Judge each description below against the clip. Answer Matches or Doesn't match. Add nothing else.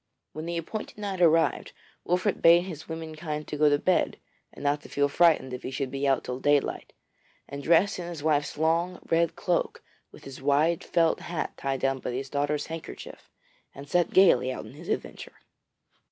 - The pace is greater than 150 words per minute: Matches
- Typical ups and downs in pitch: Matches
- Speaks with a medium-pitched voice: Matches